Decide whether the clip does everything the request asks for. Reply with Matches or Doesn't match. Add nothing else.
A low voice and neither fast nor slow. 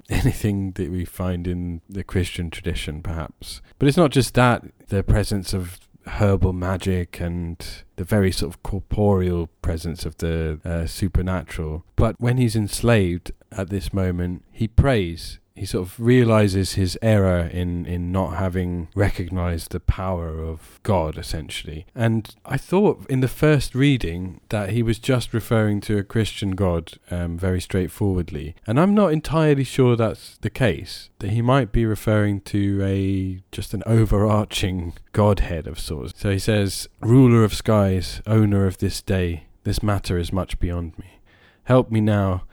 Matches